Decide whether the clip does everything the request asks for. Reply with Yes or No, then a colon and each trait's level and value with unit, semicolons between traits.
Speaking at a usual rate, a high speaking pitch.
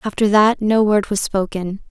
Yes: average, 190 wpm; high, 205 Hz